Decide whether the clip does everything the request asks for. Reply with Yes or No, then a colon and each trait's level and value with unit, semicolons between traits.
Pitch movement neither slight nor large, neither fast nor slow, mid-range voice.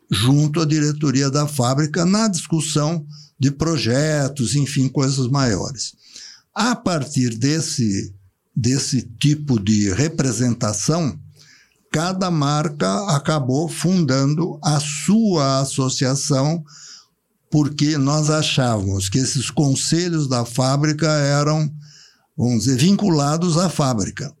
No: average, 3.2 semitones; slow, 100 wpm; medium, 145 Hz